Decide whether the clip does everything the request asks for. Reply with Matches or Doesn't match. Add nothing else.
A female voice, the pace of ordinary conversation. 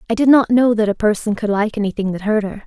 Doesn't match